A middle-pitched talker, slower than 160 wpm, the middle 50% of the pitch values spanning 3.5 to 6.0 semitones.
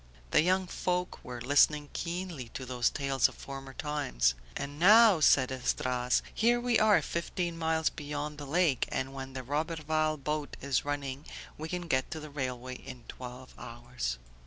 No: medium, 145 Hz; average, 165 wpm; average, 3.9 semitones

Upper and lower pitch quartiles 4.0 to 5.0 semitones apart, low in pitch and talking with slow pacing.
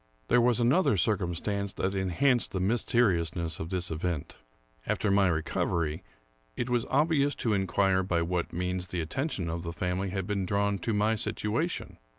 No: average, 4.3 semitones; very low, 95 Hz; average, 170 wpm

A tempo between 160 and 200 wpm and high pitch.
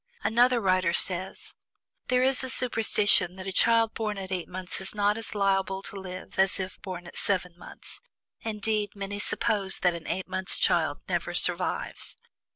Yes: average, 170 wpm; high, 195 Hz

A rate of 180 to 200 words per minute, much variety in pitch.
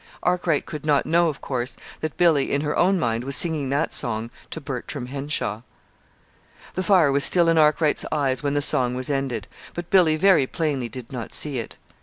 No: average, 195 wpm; average, 3.9 semitones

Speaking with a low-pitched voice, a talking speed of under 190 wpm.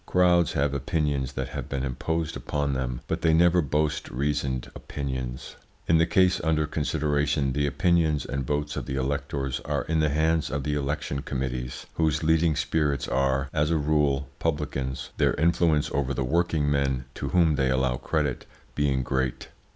Yes: very low, 75 Hz; average, 170 wpm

